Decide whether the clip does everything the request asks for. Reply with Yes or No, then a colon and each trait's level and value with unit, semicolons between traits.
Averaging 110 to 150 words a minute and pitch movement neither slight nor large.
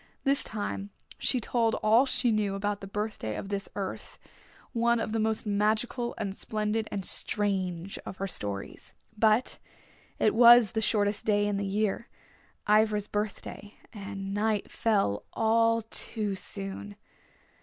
No: average, 145 wpm; narrow, 2.0 semitones